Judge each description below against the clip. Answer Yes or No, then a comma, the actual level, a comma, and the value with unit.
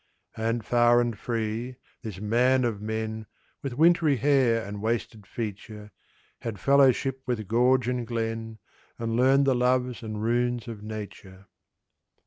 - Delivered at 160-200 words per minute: No, slow, 135 wpm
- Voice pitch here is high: No, low, 115 Hz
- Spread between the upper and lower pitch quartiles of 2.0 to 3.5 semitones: Yes, narrow, 2.5 semitones